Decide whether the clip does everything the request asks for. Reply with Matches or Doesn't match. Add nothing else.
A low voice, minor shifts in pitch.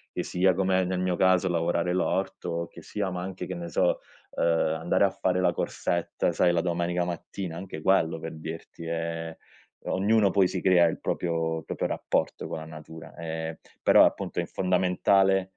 Matches